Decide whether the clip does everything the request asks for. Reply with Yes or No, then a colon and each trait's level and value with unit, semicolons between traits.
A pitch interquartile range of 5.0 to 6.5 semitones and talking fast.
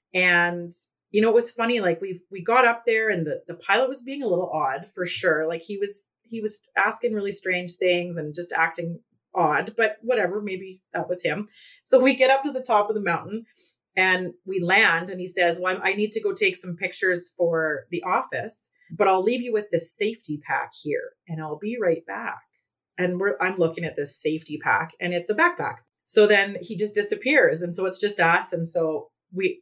No: average, 4.1 semitones; fast, 220 wpm